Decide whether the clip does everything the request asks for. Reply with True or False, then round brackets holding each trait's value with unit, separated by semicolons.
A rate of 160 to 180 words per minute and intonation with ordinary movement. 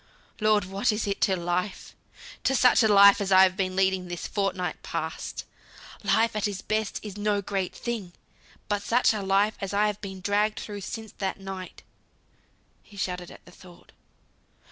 False (165 wpm; 2.0 semitones)